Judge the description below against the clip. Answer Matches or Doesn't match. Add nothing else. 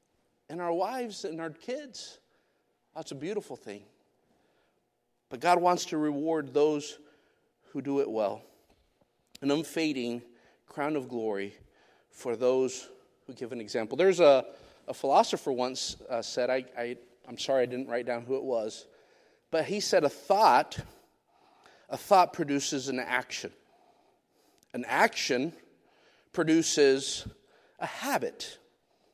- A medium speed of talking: Doesn't match